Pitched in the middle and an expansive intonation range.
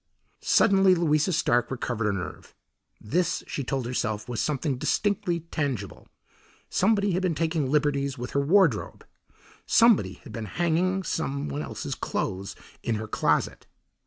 Yes: medium, 145 Hz; wide, 6.7 semitones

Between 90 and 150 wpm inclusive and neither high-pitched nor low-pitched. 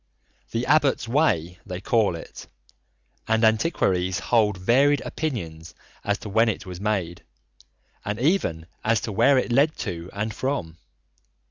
No: average, 140 wpm; low, 110 Hz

